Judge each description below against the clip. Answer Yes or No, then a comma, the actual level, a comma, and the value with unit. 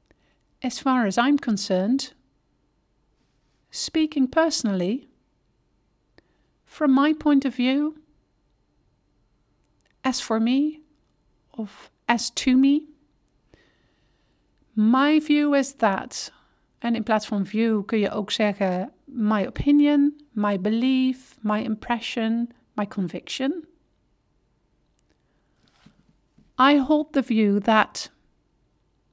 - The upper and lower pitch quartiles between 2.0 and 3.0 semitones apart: No, average, 5.0 semitones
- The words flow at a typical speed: No, slow, 90 wpm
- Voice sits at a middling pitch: No, very high, 255 Hz